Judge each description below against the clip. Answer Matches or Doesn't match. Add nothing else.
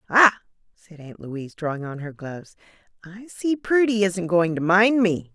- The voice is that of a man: Doesn't match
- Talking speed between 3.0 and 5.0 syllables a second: Matches